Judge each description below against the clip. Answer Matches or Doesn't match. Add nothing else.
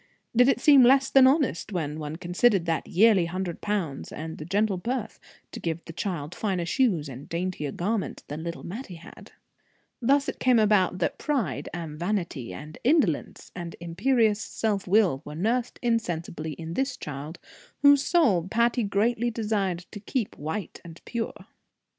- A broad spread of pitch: Matches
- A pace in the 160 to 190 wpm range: Matches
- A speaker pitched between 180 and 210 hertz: Matches